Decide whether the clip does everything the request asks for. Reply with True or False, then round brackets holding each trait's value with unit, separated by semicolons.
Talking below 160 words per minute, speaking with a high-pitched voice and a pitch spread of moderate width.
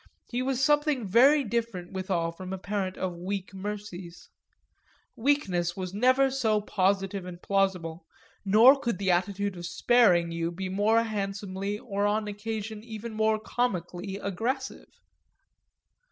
True (135 wpm; 200 Hz; 3.6 semitones)